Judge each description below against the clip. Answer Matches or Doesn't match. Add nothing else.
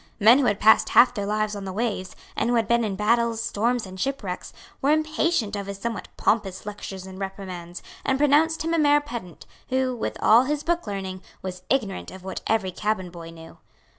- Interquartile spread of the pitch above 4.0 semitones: Matches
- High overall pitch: Matches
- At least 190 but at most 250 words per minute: Matches